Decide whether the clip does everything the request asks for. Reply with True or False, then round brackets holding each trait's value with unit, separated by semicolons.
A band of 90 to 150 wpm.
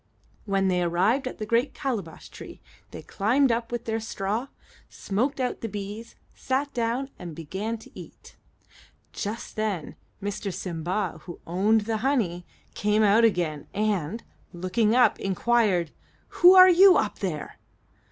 True (145 wpm)